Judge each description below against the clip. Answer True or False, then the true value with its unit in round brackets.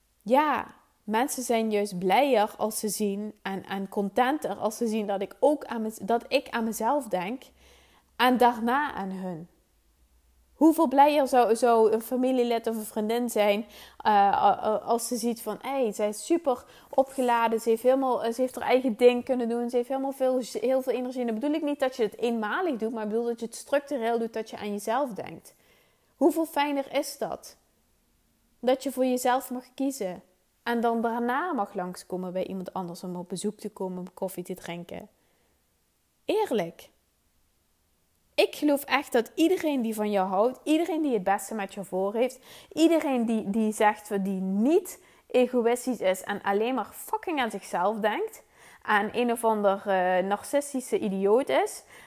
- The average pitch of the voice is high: True (230 Hz)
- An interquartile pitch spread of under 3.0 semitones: False (4.3 semitones)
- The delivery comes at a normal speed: True (180 wpm)